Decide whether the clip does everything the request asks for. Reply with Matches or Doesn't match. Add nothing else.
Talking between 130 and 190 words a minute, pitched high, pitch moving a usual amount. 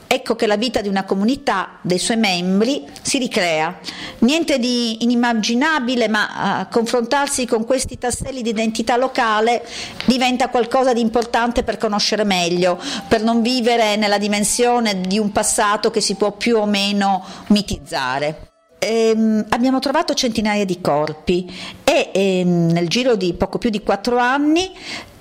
Matches